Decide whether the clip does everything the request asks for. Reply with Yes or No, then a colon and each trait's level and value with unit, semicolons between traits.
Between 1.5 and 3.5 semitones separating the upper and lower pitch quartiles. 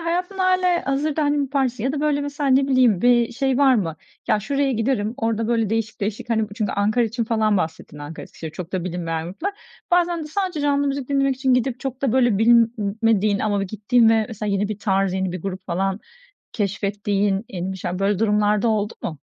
No: average, 5.3 semitones